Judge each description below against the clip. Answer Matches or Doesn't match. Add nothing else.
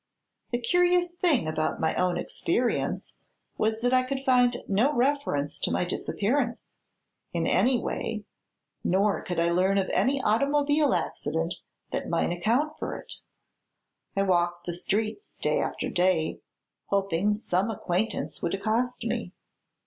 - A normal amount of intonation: Doesn't match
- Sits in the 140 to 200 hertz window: Doesn't match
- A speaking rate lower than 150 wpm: Matches